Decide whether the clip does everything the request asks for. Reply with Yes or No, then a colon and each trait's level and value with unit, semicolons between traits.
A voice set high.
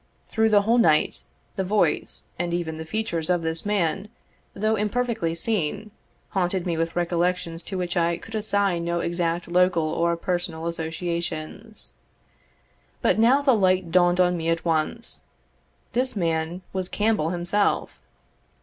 No: medium, 175 Hz